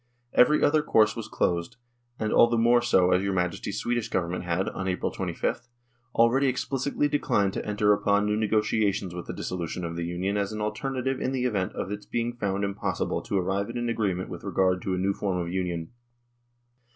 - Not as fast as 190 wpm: No, average, 200 wpm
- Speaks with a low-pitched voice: Yes, low, 100 Hz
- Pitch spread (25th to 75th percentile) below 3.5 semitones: No, average, 4.2 semitones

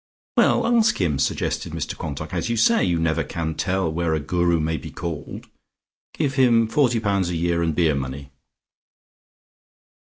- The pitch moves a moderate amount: No, wide, 5.9 semitones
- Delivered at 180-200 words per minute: No, average, 165 wpm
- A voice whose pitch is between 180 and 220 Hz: No, very low, 85 Hz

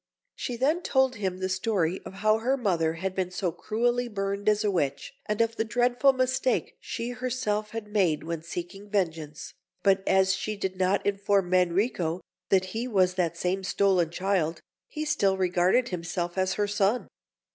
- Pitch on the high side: Yes, high, 195 Hz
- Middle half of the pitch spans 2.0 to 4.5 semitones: Yes, average, 3.8 semitones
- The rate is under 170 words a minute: No, average, 175 wpm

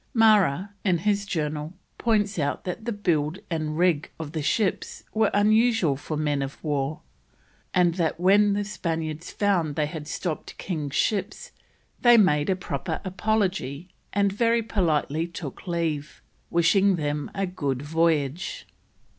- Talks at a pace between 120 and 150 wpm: Yes, average, 145 wpm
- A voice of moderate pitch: Yes, medium, 170 Hz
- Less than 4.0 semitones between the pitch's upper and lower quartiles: No, average, 4.9 semitones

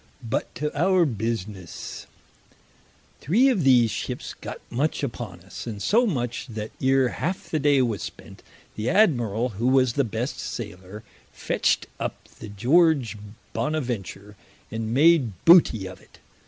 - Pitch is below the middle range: Yes, low, 120 Hz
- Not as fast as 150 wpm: Yes, average, 140 wpm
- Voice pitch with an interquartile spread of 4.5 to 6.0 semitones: Yes, wide, 5.5 semitones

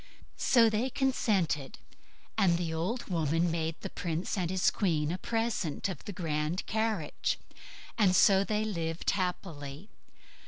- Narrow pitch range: No, average, 4.6 semitones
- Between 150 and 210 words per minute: No, slow, 135 wpm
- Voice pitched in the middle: Yes, medium, 180 Hz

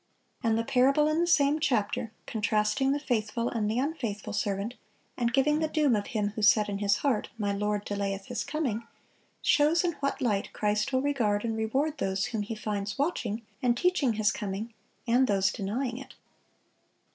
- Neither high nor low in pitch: No, high, 230 Hz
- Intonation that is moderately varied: Yes, average, 4.7 semitones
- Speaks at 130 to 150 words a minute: No, average, 180 wpm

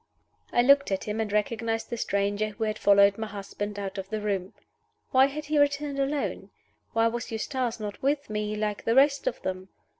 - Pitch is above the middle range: Yes, high, 220 Hz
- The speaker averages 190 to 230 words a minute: Yes, average, 200 wpm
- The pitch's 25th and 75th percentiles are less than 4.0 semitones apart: No, average, 4.7 semitones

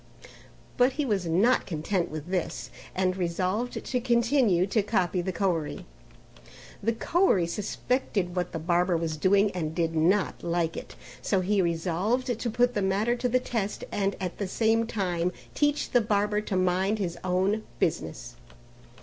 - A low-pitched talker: No, high, 190 Hz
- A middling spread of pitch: Yes, average, 4.2 semitones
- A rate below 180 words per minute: Yes, average, 160 wpm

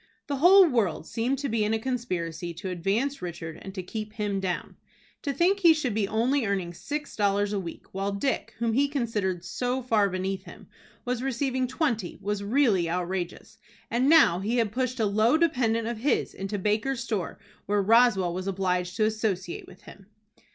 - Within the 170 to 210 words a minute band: Yes, average, 185 wpm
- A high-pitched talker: Yes, high, 215 Hz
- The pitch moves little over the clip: No, average, 4.8 semitones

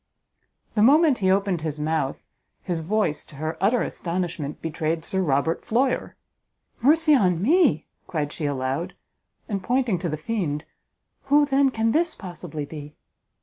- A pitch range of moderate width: No, wide, 7.4 semitones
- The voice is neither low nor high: Yes, medium, 180 Hz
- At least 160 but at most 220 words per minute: No, average, 150 wpm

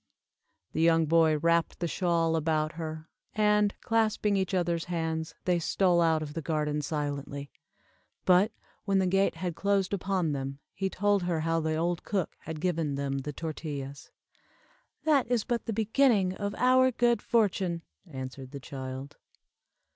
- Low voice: No, medium, 170 Hz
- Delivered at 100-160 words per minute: Yes, average, 155 wpm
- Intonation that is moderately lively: Yes, average, 4.2 semitones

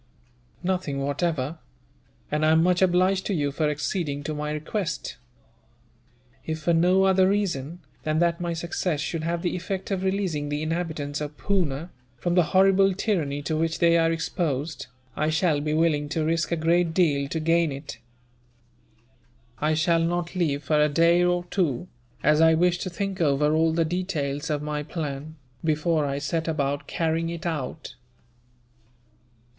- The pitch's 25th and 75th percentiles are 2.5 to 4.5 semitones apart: Yes, average, 2.8 semitones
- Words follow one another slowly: No, average, 165 wpm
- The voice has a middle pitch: Yes, medium, 165 Hz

